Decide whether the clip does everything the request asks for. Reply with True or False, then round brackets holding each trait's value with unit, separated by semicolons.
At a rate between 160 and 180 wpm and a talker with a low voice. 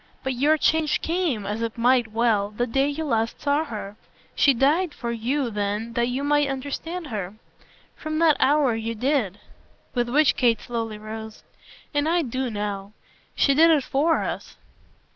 False (170 wpm; 250 Hz)